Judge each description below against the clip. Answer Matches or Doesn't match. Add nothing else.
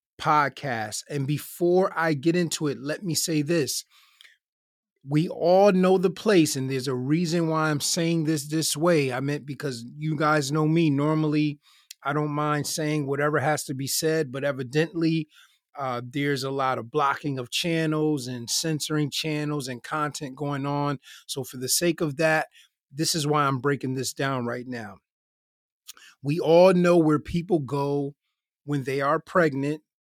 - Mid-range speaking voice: Matches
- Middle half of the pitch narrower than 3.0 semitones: Matches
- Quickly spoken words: Doesn't match